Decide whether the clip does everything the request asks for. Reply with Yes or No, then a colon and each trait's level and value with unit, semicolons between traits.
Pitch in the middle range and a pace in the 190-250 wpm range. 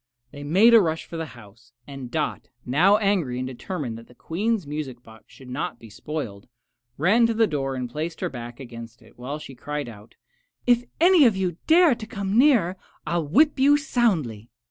Yes: medium, 150 Hz; average, 200 wpm